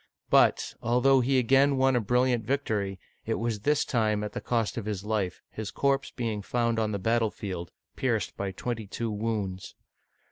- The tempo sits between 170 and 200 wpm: Yes, average, 175 wpm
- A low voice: Yes, low, 115 Hz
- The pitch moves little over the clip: No, average, 3.1 semitones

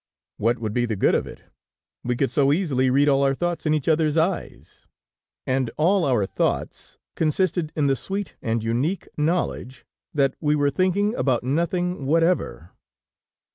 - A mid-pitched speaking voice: Yes, medium, 145 Hz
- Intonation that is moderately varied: Yes, average, 4.9 semitones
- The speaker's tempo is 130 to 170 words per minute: Yes, average, 165 wpm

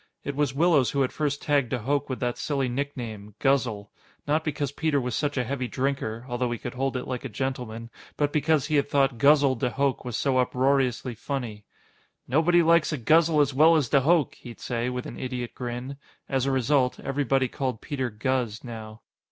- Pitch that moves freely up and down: No, average, 2.7 semitones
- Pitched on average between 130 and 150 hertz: Yes, low, 135 Hz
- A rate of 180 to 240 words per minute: Yes, average, 200 wpm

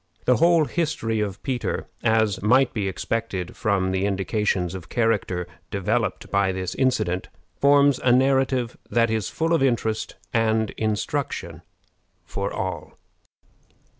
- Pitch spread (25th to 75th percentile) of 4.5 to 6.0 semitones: Yes, average, 5.0 semitones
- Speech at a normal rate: No, slow, 130 wpm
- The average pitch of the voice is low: Yes, low, 110 Hz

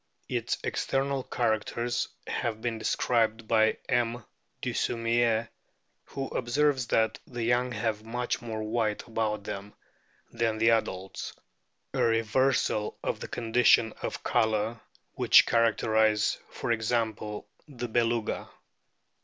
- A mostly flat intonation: Yes, narrow, 1.6 semitones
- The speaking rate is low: Yes, slow, 110 wpm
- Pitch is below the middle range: Yes, low, 115 Hz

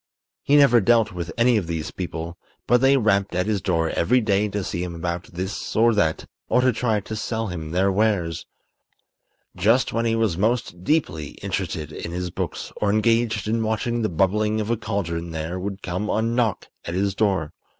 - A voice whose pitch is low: Yes, low, 100 Hz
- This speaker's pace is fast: No, average, 195 wpm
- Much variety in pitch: No, average, 4.4 semitones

